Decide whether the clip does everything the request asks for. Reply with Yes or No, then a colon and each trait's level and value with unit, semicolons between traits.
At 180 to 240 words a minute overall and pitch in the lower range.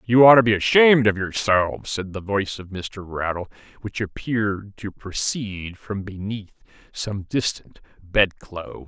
No: average, 155 wpm; low, 100 Hz